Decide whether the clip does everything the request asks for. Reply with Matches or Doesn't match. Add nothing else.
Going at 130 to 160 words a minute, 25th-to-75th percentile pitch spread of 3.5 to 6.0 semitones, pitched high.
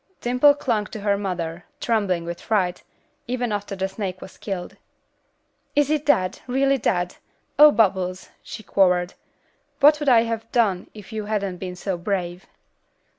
Matches